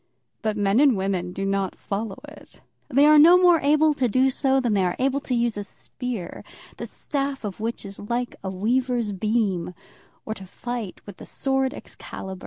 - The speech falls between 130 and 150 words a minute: No, average, 190 wpm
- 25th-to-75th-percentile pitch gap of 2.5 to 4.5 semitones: No, average, 5.2 semitones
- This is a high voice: Yes, high, 235 Hz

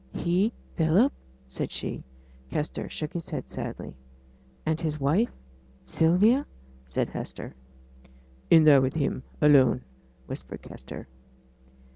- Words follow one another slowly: Yes, slow, 110 wpm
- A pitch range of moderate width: Yes, average, 4.2 semitones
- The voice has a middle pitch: Yes, medium, 160 Hz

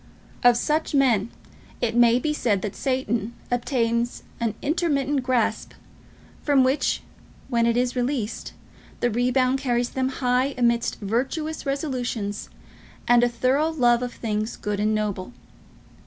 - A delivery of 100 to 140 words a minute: Yes, slow, 135 wpm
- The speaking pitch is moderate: No, high, 245 Hz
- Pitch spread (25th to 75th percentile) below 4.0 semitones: Yes, narrow, 2.4 semitones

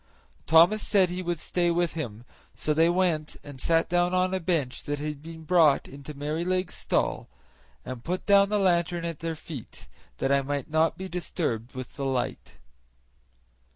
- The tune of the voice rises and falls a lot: No, average, 3.6 semitones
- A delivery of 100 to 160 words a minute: No, average, 175 wpm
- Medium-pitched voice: Yes, medium, 165 Hz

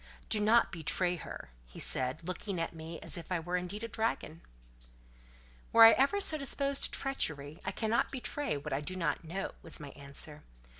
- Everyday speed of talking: Yes, average, 190 wpm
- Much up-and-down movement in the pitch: Yes, wide, 6.5 semitones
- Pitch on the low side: No, medium, 180 Hz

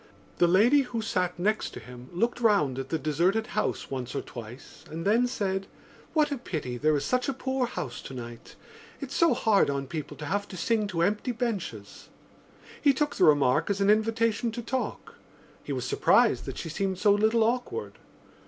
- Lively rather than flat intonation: Yes, wide, 7.5 semitones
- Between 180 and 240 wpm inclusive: Yes, average, 190 wpm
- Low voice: No, high, 200 Hz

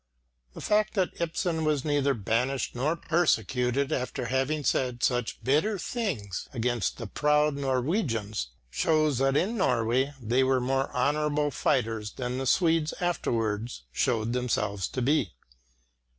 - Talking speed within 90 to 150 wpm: Yes, slow, 135 wpm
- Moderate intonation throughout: Yes, average, 4.2 semitones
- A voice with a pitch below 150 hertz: Yes, low, 135 Hz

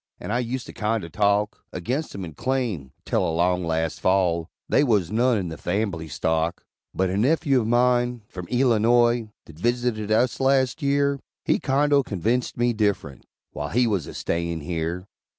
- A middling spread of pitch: No, wide, 6.0 semitones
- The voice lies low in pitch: Yes, low, 110 Hz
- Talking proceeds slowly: No, average, 170 wpm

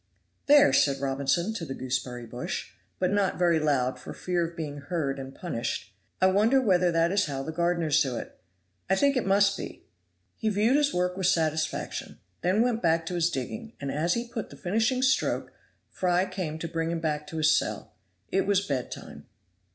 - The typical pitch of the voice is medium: Yes, medium, 170 Hz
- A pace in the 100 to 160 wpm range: No, average, 195 wpm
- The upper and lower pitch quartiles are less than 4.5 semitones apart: No, average, 5.1 semitones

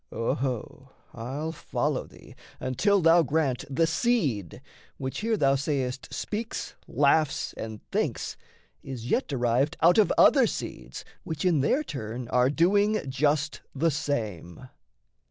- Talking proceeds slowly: Yes, slow, 130 wpm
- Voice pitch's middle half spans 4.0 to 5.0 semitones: Yes, average, 4.5 semitones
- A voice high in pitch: No, medium, 140 Hz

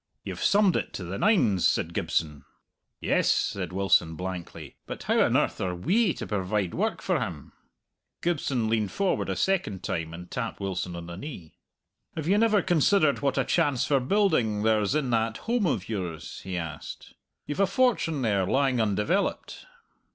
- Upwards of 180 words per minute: No, average, 175 wpm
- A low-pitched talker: Yes, low, 115 Hz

